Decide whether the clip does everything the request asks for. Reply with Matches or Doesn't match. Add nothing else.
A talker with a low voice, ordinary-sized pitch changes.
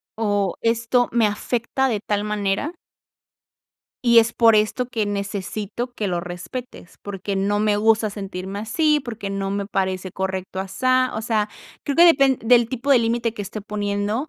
Doesn't match